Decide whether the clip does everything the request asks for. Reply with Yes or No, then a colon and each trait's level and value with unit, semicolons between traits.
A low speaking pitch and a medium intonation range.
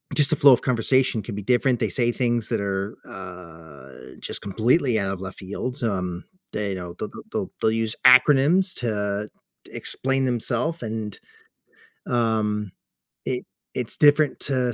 Yes: low, 115 Hz; average, 4.4 semitones